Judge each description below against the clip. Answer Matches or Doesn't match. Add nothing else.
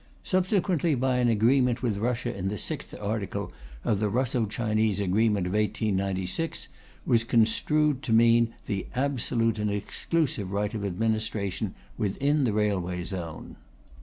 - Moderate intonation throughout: Matches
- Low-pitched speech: Matches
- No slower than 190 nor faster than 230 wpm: Doesn't match